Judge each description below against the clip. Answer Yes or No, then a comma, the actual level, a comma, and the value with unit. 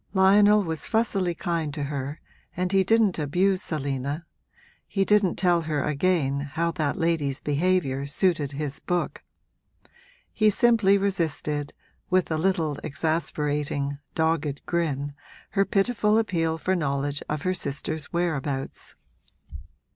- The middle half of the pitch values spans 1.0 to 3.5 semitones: No, average, 4.5 semitones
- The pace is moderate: No, slow, 125 wpm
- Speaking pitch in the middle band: Yes, medium, 165 Hz